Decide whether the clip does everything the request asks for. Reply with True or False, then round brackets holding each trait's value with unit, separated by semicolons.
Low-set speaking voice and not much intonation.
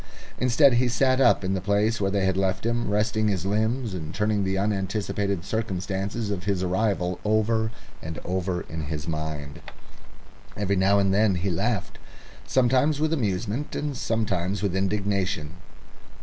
False (100 Hz; 3.1 semitones)